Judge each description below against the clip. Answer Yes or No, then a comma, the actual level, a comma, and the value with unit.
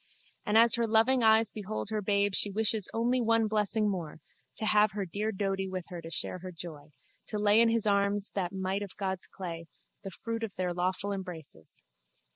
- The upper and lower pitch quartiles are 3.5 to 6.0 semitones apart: No, average, 2.9 semitones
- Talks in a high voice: Yes, high, 200 Hz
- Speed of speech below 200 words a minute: No, fast, 205 wpm